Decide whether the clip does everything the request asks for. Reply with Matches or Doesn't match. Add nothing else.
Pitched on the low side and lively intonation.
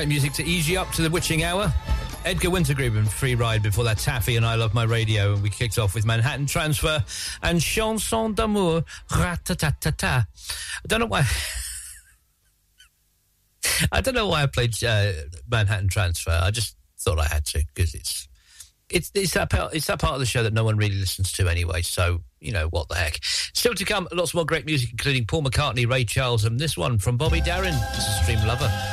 Matches